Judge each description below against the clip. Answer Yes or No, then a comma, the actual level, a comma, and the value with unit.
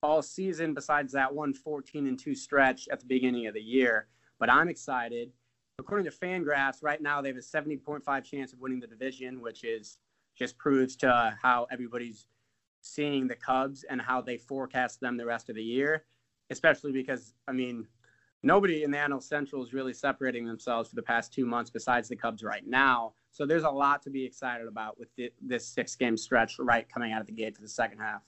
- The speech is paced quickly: Yes, fast, 215 wpm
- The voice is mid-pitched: No, low, 130 Hz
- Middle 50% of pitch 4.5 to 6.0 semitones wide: No, average, 3.0 semitones